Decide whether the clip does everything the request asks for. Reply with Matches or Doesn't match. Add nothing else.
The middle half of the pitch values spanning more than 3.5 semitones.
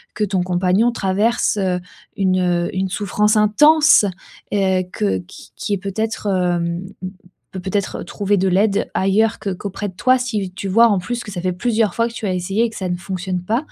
Doesn't match